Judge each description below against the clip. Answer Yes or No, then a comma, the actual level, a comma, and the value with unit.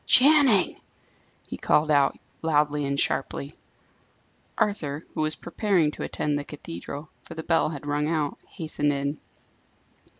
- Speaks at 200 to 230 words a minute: No, slow, 135 wpm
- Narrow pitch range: Yes, narrow, 2.2 semitones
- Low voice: No, medium, 150 Hz